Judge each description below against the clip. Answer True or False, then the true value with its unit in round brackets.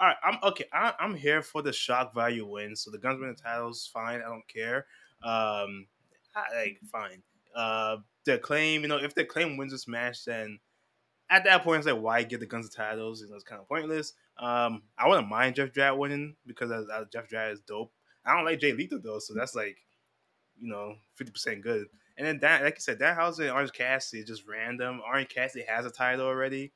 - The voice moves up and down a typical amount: True (4.0 semitones)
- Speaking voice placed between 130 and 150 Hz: False (120 Hz)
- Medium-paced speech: False (220 wpm)